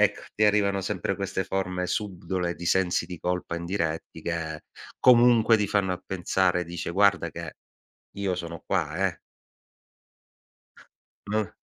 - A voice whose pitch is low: Yes, very low, 95 Hz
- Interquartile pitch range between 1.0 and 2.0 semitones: No, narrow, 2.6 semitones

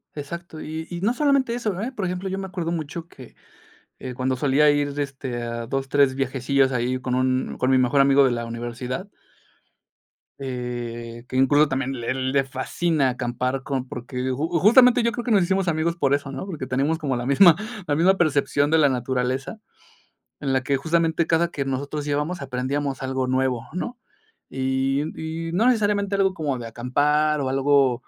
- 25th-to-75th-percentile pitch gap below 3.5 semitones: No, average, 4.3 semitones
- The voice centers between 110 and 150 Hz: Yes, medium, 140 Hz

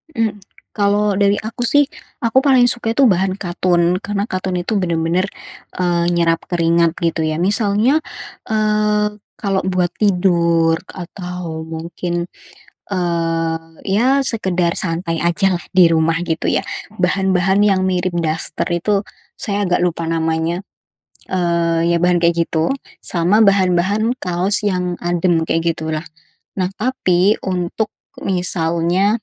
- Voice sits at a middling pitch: Yes, medium, 180 Hz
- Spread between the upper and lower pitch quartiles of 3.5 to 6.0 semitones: No, average, 3.1 semitones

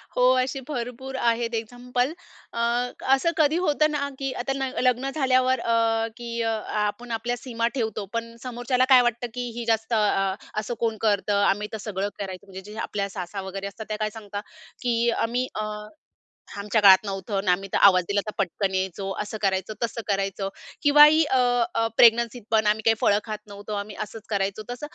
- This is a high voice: Yes, high, 225 Hz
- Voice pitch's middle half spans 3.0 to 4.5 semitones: Yes, average, 3.4 semitones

